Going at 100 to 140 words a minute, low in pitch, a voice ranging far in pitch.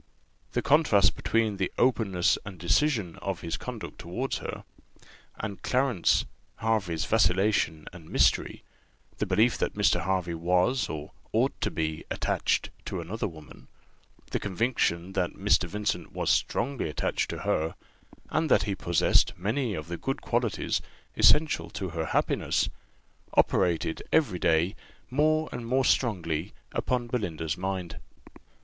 Yes: slow, 135 wpm; very low, 95 Hz; wide, 5.7 semitones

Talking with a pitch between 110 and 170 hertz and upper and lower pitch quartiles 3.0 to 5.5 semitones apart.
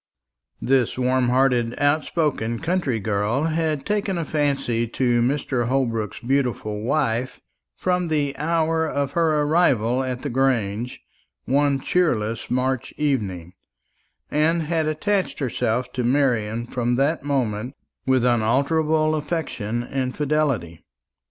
Yes: low, 135 Hz; average, 4.4 semitones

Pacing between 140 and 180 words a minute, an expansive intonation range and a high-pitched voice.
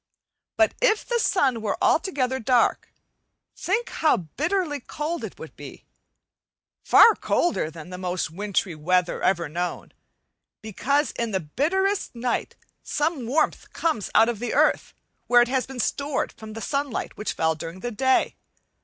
Yes: average, 155 wpm; wide, 8.1 semitones; high, 245 Hz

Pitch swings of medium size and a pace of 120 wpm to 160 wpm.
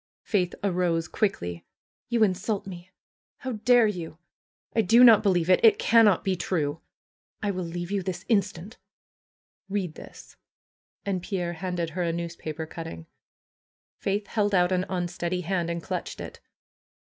Yes: average, 3.0 semitones; average, 150 wpm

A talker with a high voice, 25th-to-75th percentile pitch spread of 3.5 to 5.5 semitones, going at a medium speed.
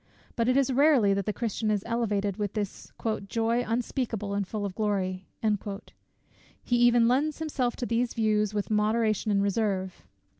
No: high, 215 Hz; average, 2.9 semitones; average, 160 wpm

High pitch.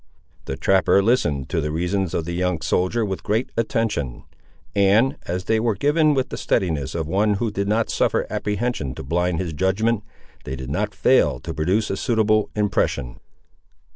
No: very low, 95 Hz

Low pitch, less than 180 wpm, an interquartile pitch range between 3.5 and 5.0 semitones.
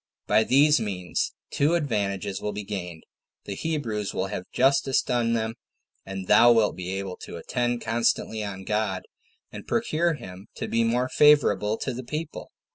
Yes: low, 110 Hz; average, 165 wpm; average, 4.7 semitones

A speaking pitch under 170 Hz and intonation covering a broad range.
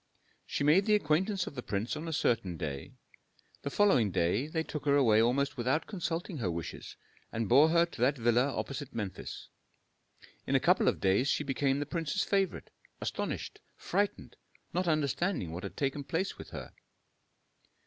Yes: medium, 140 Hz; wide, 6.0 semitones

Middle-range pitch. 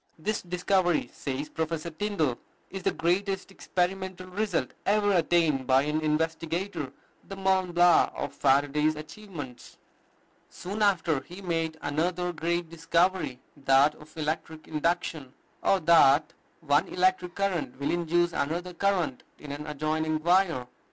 Yes: medium, 165 Hz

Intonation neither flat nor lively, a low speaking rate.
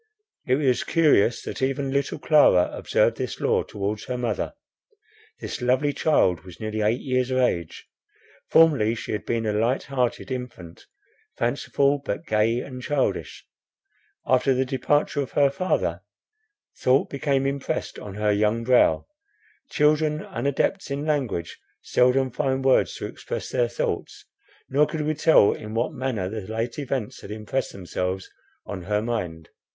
No: average, 4.5 semitones; average, 150 wpm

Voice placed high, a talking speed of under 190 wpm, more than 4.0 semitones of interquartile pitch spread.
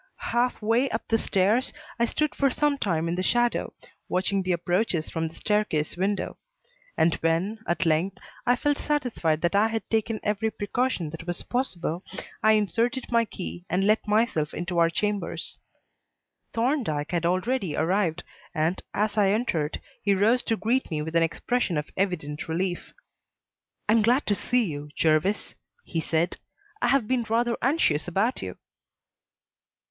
Yes: high, 200 Hz; average, 165 wpm; wide, 5.6 semitones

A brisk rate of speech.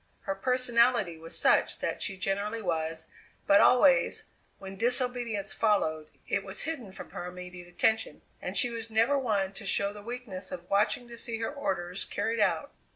No: average, 170 wpm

